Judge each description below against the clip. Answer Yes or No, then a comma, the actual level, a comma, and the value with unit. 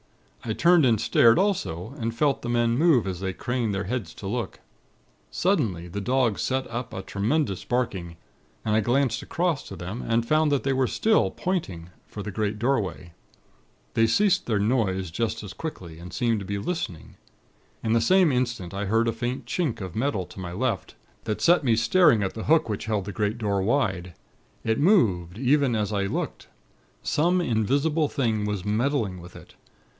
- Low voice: Yes, low, 115 Hz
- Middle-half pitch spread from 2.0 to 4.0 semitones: No, wide, 5.5 semitones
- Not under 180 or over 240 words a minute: Yes, average, 185 wpm